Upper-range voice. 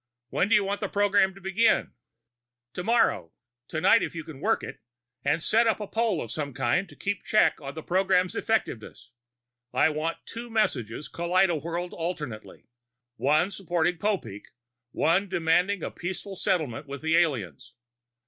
No: medium, 175 Hz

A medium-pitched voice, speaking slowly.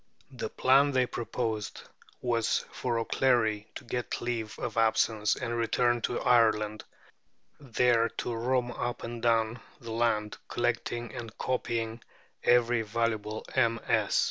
No: low, 115 Hz; slow, 125 wpm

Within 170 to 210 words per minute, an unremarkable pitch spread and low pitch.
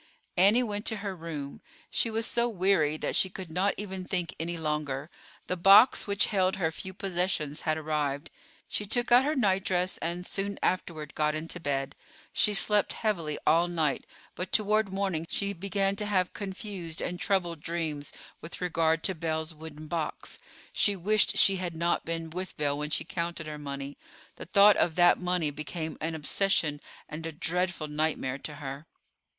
No: average, 175 wpm; average, 3.9 semitones; medium, 175 Hz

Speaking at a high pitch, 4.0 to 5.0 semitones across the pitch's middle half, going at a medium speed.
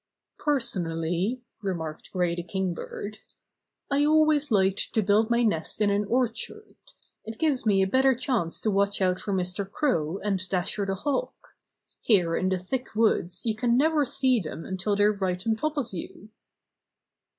Yes: high, 205 Hz; average, 4.7 semitones; average, 165 wpm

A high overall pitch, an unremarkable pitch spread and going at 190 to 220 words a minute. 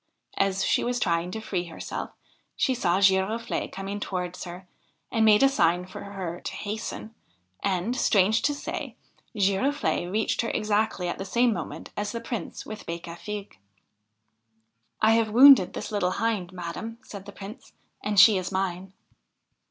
No: high, 200 Hz; average, 3.5 semitones; average, 160 wpm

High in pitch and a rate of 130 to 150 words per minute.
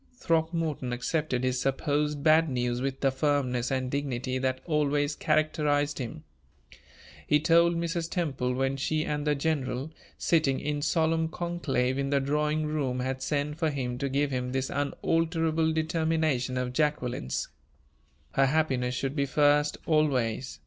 No: medium, 145 Hz; average, 145 wpm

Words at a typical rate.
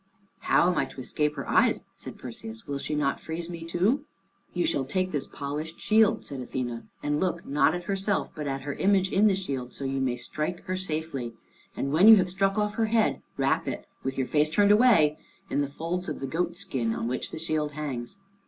No: fast, 225 wpm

